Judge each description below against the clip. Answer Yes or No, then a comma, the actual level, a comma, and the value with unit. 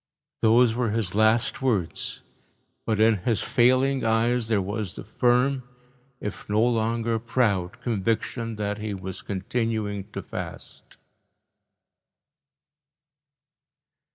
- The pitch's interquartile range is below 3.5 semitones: Yes, narrow, 2.5 semitones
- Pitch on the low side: Yes, low, 110 Hz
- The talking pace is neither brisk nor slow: No, slow, 105 wpm